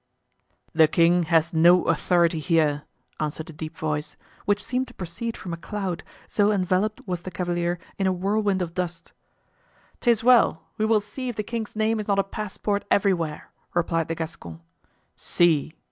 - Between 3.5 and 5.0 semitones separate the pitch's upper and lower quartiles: Yes, average, 3.9 semitones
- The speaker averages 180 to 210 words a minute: No, average, 170 wpm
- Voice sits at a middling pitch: Yes, medium, 180 Hz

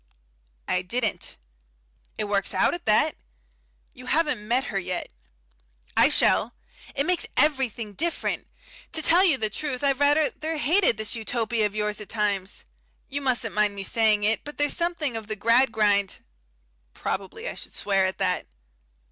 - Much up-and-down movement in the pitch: Yes, wide, 5.7 semitones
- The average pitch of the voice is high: Yes, high, 225 Hz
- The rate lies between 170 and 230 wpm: No, average, 160 wpm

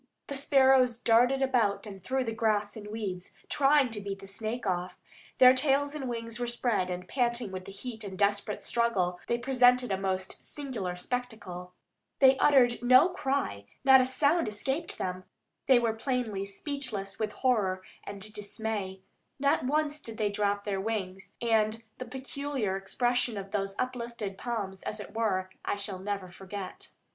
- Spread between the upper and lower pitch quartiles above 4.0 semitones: Yes, average, 4.5 semitones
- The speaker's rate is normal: Yes, average, 170 wpm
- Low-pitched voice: No, high, 225 Hz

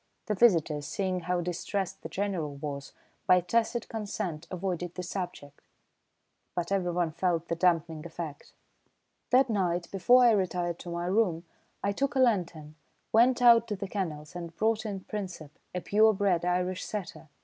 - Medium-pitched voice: Yes, medium, 180 Hz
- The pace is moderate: Yes, average, 160 wpm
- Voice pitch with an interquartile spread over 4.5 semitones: No, average, 3.3 semitones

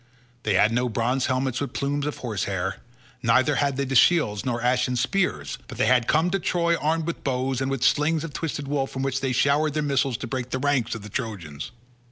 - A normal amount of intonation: Yes, average, 3.2 semitones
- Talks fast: Yes, fast, 225 wpm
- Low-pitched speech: Yes, low, 130 Hz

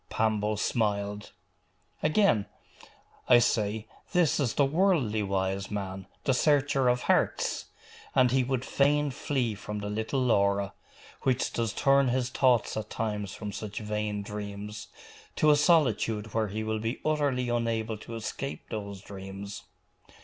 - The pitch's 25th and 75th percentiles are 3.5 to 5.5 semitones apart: Yes, average, 4.2 semitones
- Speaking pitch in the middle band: No, low, 110 Hz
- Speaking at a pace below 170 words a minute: Yes, average, 140 wpm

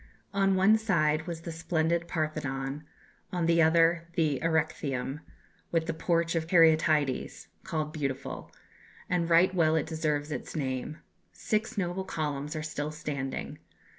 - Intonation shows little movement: Yes, narrow, 2.0 semitones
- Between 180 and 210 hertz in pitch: No, medium, 160 Hz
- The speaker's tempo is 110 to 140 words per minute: Yes, slow, 135 wpm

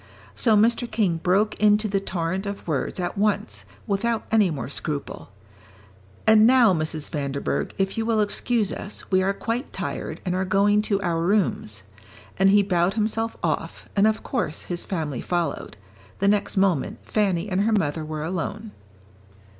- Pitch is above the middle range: Yes, high, 195 Hz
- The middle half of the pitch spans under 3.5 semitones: No, average, 4.1 semitones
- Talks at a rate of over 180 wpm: No, average, 165 wpm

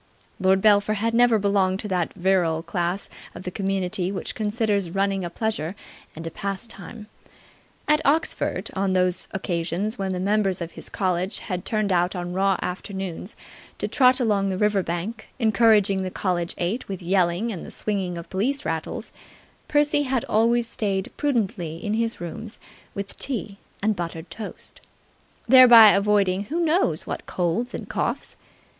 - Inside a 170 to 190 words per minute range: No, average, 160 wpm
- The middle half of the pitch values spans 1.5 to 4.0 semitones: Yes, average, 3.3 semitones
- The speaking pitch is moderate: No, high, 195 Hz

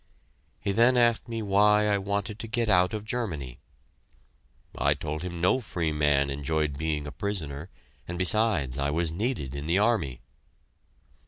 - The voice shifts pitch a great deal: Yes, wide, 6.2 semitones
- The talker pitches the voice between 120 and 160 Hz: No, very low, 90 Hz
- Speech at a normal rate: Yes, average, 160 wpm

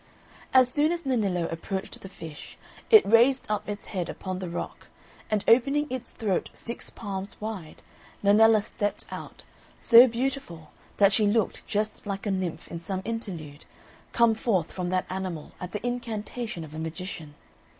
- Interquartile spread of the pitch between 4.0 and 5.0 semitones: Yes, average, 4.3 semitones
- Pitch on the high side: Yes, high, 205 Hz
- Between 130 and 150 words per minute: No, average, 160 wpm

